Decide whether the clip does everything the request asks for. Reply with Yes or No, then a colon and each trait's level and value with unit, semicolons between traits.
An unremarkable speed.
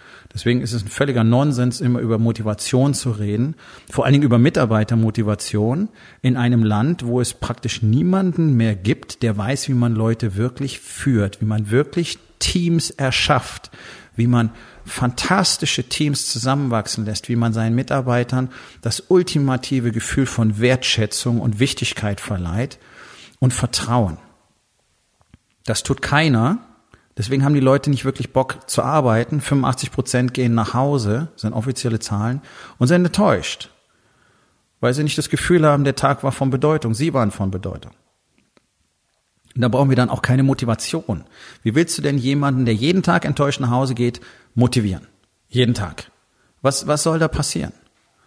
Yes: average, 155 wpm